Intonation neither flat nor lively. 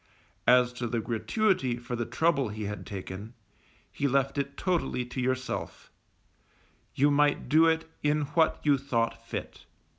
Yes: average, 3.7 semitones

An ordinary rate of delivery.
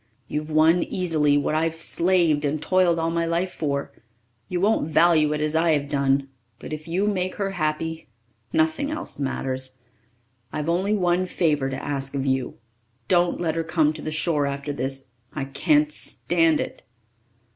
Yes: average, 170 wpm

